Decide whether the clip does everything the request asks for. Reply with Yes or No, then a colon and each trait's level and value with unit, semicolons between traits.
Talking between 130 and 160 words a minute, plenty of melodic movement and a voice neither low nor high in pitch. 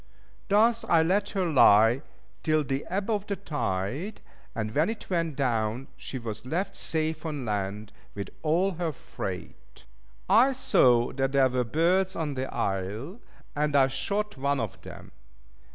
Yes: average, 155 wpm; wide, 7.4 semitones; medium, 145 Hz